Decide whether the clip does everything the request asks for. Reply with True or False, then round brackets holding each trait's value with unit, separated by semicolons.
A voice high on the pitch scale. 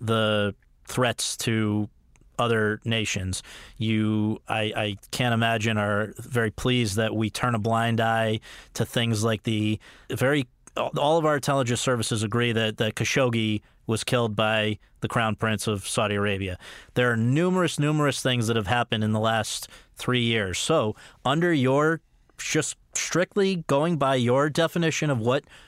False (115 Hz)